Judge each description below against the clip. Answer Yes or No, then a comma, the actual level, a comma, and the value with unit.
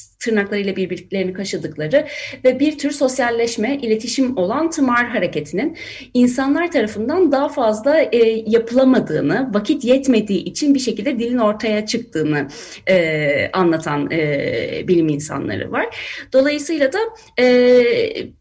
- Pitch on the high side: Yes, high, 235 Hz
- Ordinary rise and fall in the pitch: No, wide, 6.7 semitones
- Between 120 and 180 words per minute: No, average, 110 wpm